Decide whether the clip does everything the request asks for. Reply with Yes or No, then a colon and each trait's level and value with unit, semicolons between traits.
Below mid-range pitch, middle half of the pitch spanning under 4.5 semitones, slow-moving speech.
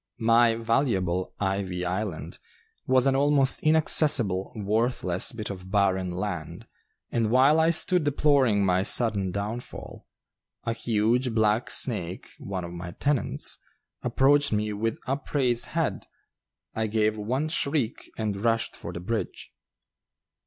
No: low, 110 Hz; average, 4.9 semitones; slow, 125 wpm